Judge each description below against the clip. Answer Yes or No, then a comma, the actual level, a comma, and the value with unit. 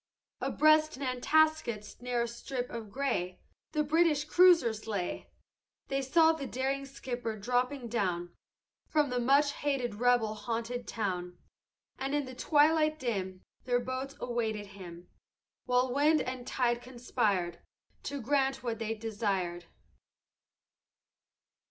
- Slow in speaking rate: Yes, slow, 120 wpm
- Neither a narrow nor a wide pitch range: Yes, average, 4.1 semitones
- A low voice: No, high, 245 Hz